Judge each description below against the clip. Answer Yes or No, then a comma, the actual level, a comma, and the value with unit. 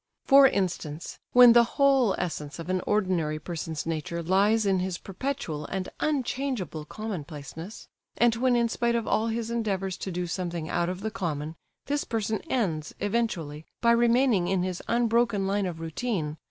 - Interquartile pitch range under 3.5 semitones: No, wide, 5.6 semitones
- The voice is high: Yes, high, 195 Hz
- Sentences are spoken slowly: No, average, 165 wpm